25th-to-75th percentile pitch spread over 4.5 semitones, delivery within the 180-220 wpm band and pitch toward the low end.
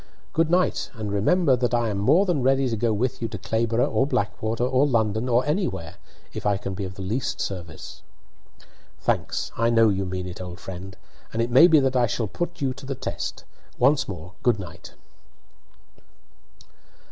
Yes: average, 5.1 semitones; average, 190 wpm; low, 115 Hz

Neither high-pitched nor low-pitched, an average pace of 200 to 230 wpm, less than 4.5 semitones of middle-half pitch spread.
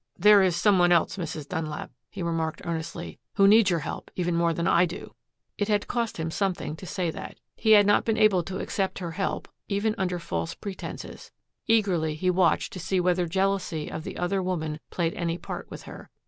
Yes: medium, 180 Hz; fast, 205 wpm; average, 2.9 semitones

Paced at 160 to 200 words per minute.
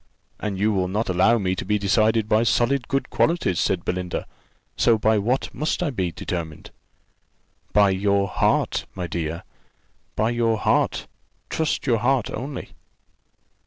No: average, 150 wpm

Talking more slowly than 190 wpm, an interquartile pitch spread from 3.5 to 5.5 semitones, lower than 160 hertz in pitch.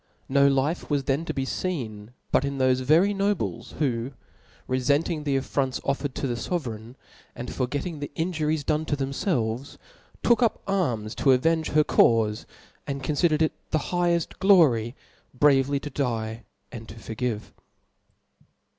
Yes: average, 155 wpm; average, 4.1 semitones; medium, 140 Hz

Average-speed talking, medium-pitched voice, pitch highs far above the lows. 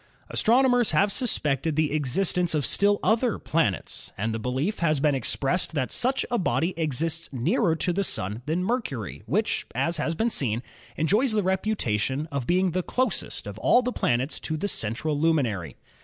Yes: average, 170 wpm; medium, 160 Hz; wide, 7.2 semitones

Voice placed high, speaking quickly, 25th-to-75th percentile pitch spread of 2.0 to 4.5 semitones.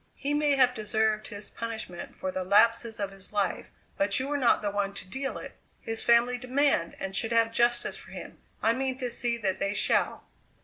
Yes: high, 230 Hz; fast, 210 wpm; average, 3.6 semitones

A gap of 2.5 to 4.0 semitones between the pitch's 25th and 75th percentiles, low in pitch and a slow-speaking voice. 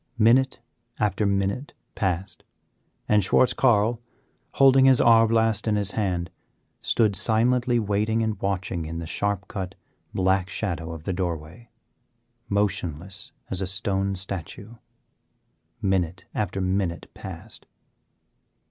Yes: average, 3.2 semitones; low, 100 Hz; slow, 115 wpm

